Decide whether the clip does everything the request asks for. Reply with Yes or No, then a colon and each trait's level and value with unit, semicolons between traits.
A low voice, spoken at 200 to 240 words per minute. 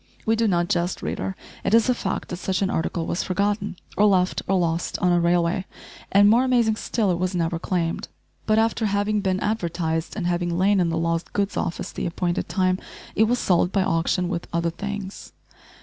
No: medium, 185 Hz; fast, 205 wpm